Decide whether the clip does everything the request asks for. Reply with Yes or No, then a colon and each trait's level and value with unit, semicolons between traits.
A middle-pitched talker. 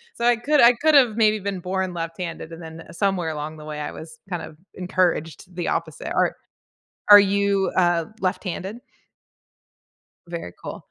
Yes: medium, 180 Hz